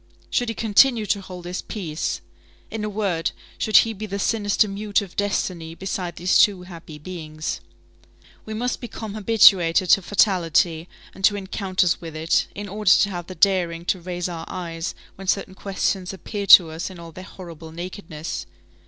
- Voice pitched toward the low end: No, medium, 185 Hz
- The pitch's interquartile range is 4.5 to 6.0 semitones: No, average, 3.2 semitones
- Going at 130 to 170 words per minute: No, average, 180 wpm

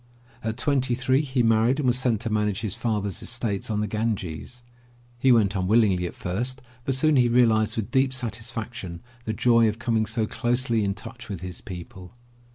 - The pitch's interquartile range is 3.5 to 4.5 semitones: No, average, 3.1 semitones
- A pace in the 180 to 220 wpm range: Yes, average, 185 wpm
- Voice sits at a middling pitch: No, low, 115 Hz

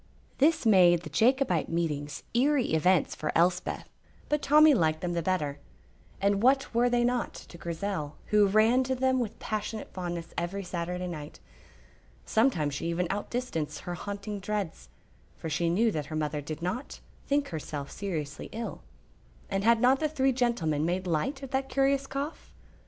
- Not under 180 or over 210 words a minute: No, average, 165 wpm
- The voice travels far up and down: Yes, wide, 7.0 semitones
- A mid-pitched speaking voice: No, high, 195 Hz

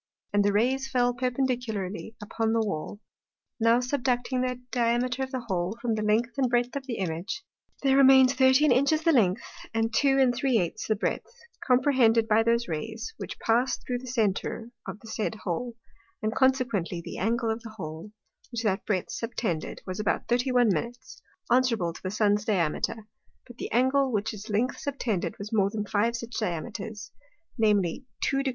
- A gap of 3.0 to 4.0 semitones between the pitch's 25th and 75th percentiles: Yes, average, 3.4 semitones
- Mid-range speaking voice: No, high, 230 Hz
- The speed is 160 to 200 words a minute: Yes, average, 170 wpm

